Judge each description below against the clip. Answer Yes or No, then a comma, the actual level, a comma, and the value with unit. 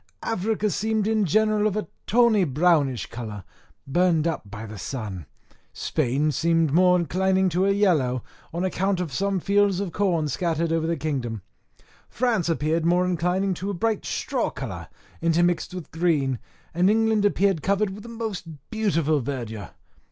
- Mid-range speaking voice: Yes, medium, 175 Hz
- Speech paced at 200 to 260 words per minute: No, average, 160 wpm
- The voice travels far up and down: No, average, 4.7 semitones